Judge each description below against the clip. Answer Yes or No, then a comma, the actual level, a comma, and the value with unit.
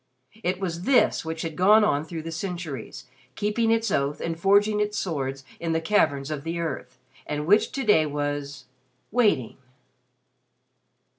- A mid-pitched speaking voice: Yes, medium, 165 Hz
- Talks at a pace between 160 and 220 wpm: No, average, 150 wpm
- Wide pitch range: Yes, wide, 5.9 semitones